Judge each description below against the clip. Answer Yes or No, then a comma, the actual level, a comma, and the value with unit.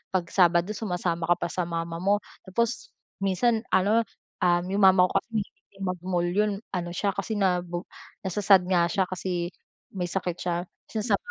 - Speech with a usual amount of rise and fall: No, narrow, 2.2 semitones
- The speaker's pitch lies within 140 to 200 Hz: Yes, medium, 185 Hz